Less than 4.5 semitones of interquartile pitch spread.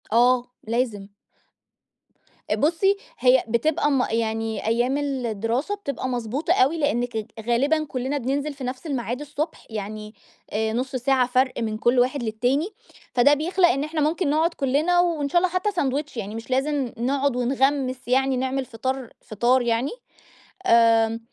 Yes: average, 3.6 semitones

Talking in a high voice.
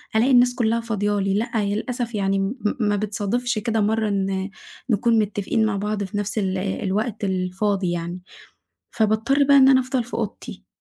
Yes: high, 210 Hz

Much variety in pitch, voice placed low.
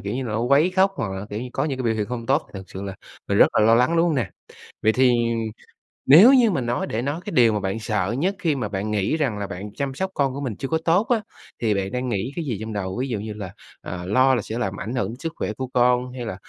No: average, 4.9 semitones; low, 120 Hz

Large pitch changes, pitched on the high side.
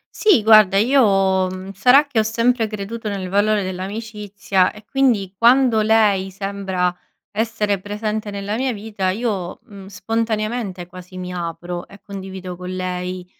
No: average, 2.9 semitones; high, 200 Hz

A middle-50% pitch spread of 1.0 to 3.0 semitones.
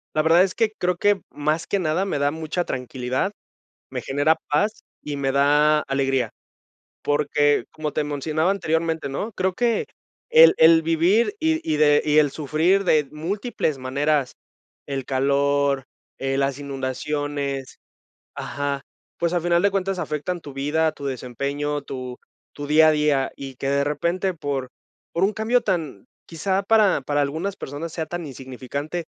No: average, 3.8 semitones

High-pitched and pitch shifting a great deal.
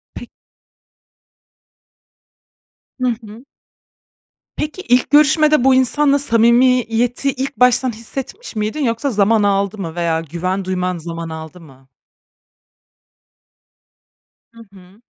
Yes: high, 225 Hz; wide, 6.1 semitones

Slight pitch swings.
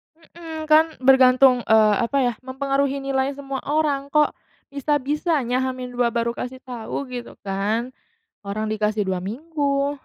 No: average, 3.1 semitones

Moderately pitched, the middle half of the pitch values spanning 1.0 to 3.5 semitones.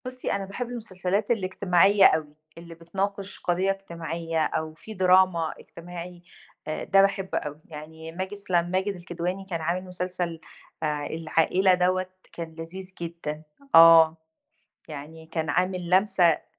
Yes: medium, 175 Hz; narrow, 2.6 semitones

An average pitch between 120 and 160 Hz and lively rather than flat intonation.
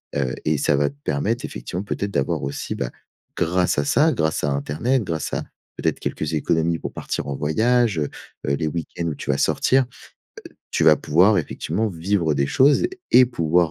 No: very low, 80 Hz; wide, 6.0 semitones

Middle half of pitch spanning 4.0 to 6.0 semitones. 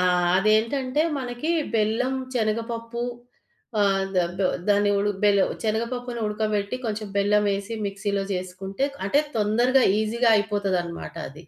No: average, 2.7 semitones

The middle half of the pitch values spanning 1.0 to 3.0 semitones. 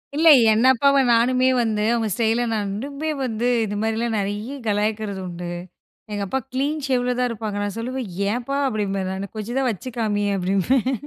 No: average, 3.7 semitones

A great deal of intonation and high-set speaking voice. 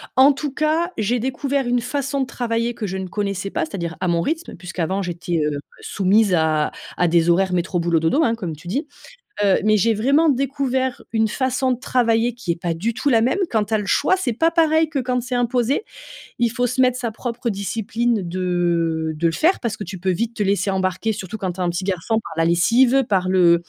Yes: wide, 5.9 semitones; high, 220 Hz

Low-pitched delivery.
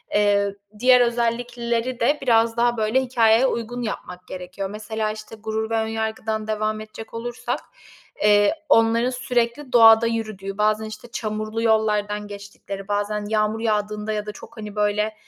No: high, 220 Hz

